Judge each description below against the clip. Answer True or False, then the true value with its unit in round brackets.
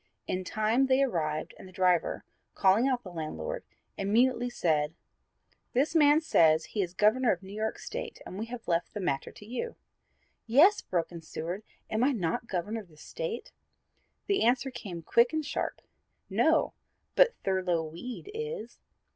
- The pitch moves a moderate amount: False (6.7 semitones)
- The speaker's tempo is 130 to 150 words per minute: False (165 wpm)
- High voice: True (215 Hz)